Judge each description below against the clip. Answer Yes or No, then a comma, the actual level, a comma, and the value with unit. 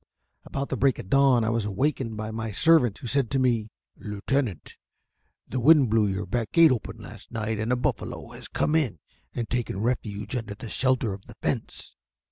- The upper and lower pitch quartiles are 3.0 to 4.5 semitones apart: Yes, average, 3.5 semitones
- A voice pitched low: Yes, low, 115 Hz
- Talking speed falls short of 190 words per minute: No, average, 195 wpm